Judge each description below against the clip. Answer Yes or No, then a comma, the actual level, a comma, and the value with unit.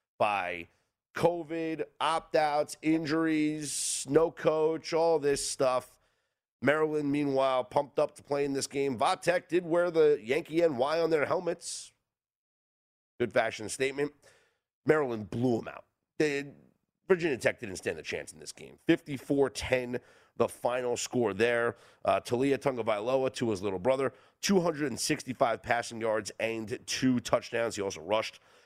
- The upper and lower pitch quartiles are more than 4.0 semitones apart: Yes, average, 4.9 semitones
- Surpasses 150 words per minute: No, average, 140 wpm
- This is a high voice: No, medium, 140 Hz